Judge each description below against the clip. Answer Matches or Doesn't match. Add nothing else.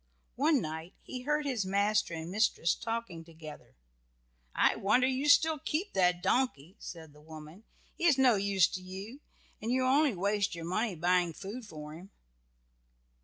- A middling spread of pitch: Doesn't match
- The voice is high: Matches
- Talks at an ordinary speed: Matches